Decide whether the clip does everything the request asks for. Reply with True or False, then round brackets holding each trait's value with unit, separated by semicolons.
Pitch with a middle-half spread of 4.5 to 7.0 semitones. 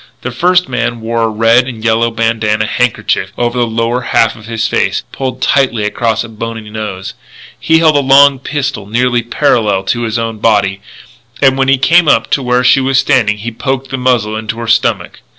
False (2.9 semitones)